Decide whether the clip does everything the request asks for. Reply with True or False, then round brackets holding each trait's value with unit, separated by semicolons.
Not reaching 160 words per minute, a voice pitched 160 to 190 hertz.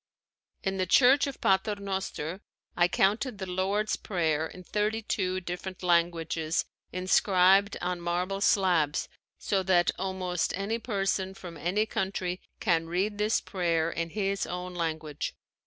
True (140 wpm; 185 Hz)